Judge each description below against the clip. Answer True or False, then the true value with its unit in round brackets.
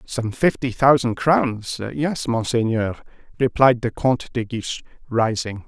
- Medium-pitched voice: False (120 Hz)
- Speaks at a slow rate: True (125 wpm)